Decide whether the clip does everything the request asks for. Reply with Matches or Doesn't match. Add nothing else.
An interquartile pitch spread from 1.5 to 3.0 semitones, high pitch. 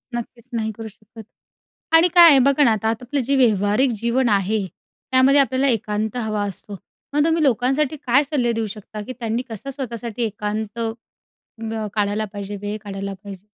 Doesn't match